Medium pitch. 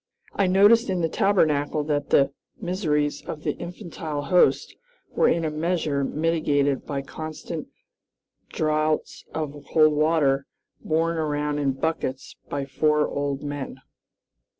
Yes: medium, 155 Hz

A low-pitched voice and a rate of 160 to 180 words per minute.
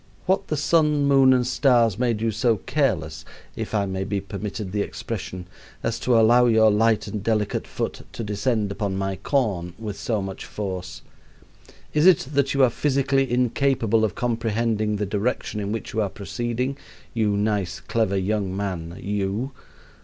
Yes: low, 110 Hz; average, 170 wpm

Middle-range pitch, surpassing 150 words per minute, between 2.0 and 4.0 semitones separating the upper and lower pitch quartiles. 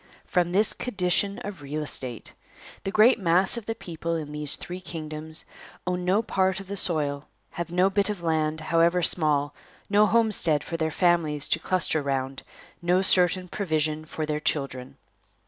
Yes: medium, 170 Hz; average, 165 wpm; average, 3.6 semitones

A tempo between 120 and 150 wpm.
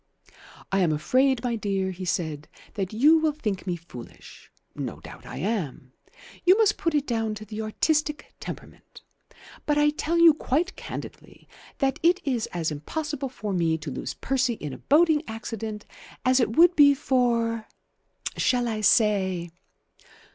No: average, 160 wpm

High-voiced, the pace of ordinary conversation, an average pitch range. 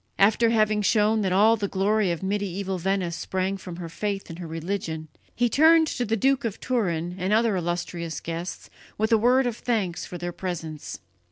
Yes: high, 195 Hz; average, 195 wpm; average, 3.9 semitones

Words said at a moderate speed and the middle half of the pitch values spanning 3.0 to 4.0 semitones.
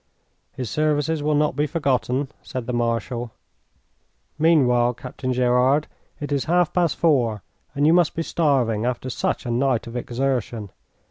Yes: average, 150 wpm; average, 3.7 semitones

